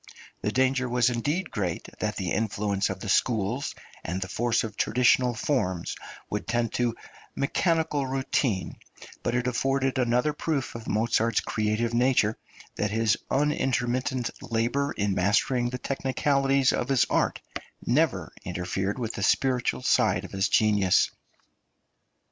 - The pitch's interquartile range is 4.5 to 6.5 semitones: No, average, 4.0 semitones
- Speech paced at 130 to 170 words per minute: Yes, slow, 135 wpm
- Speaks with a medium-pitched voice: No, low, 120 Hz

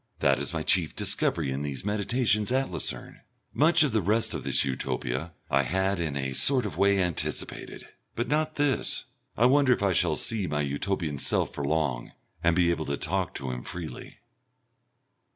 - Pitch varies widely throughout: Yes, wide, 7.4 semitones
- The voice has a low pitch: Yes, very low, 90 Hz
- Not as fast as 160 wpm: No, average, 185 wpm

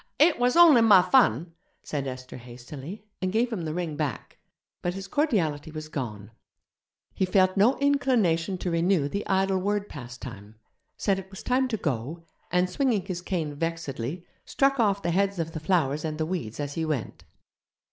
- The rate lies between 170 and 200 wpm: Yes, average, 175 wpm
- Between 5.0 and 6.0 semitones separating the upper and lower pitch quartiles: Yes, average, 5.3 semitones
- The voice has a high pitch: No, medium, 175 Hz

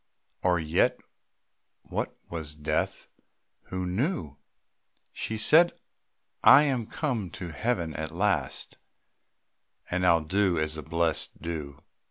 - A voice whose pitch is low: Yes, very low, 85 Hz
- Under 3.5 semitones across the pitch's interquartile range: No, average, 5.3 semitones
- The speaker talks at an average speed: No, slow, 120 wpm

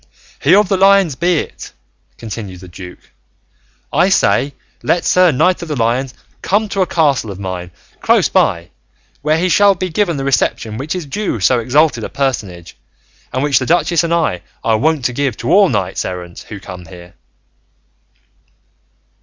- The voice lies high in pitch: No, medium, 140 Hz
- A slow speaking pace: No, average, 180 wpm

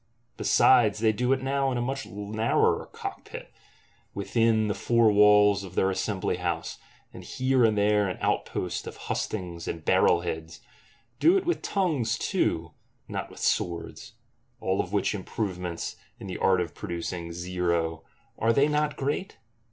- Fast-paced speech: No, average, 150 wpm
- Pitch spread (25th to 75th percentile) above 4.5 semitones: Yes, average, 5.2 semitones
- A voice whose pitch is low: Yes, low, 105 Hz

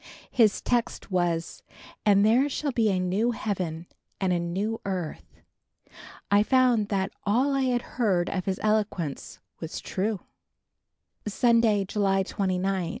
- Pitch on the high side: Yes, high, 200 Hz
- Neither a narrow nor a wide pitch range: Yes, average, 3.6 semitones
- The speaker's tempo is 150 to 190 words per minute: No, slow, 135 wpm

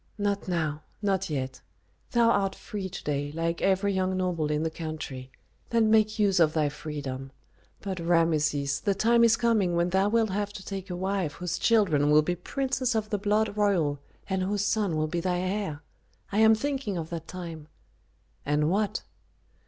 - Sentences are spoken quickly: No, average, 185 wpm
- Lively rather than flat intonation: No, average, 4.7 semitones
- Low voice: No, medium, 185 Hz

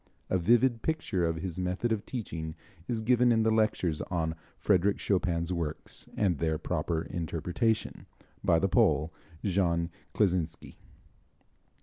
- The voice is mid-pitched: No, very low, 90 Hz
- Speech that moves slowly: Yes, slow, 130 wpm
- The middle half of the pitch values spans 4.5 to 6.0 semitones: Yes, average, 4.8 semitones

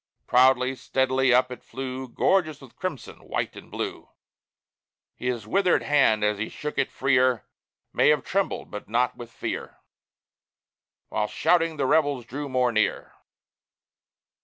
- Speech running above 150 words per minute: No, slow, 135 wpm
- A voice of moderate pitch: No, low, 130 Hz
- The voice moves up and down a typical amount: Yes, average, 3.2 semitones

